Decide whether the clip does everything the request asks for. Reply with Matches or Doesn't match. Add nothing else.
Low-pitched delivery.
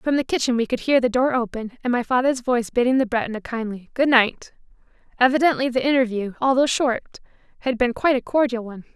Doesn't match